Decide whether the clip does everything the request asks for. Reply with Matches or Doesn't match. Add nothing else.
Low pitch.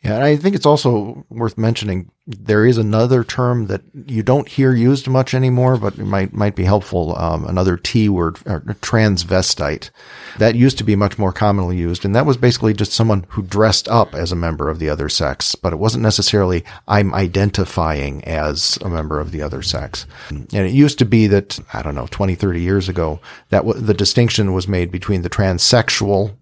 Matches